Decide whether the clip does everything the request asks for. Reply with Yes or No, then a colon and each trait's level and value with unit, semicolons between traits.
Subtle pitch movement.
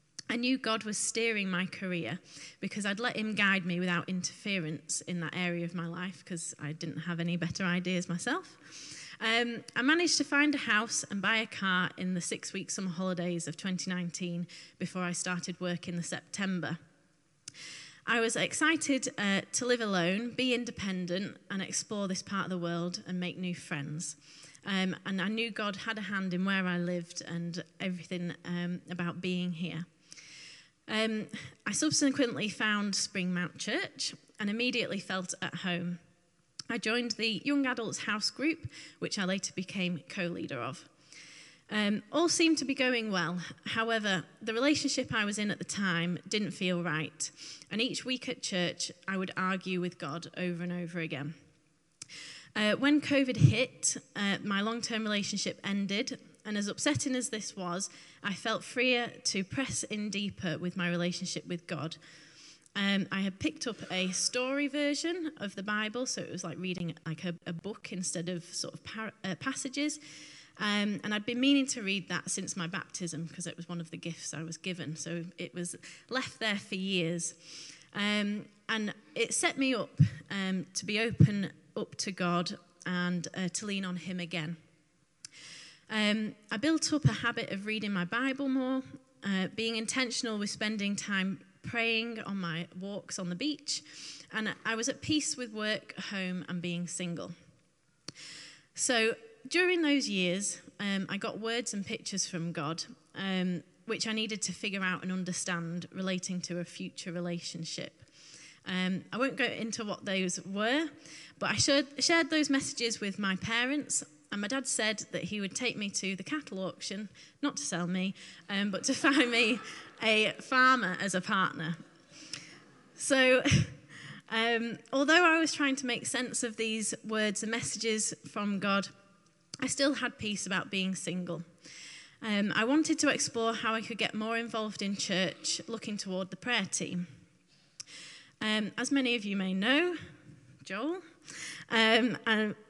No: average, 4.5 semitones